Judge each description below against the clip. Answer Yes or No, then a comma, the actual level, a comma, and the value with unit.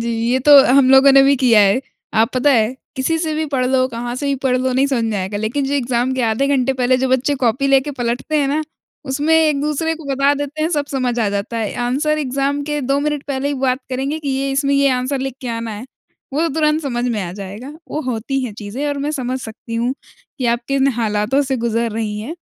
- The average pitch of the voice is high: Yes, very high, 265 Hz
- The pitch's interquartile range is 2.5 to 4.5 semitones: Yes, average, 3.1 semitones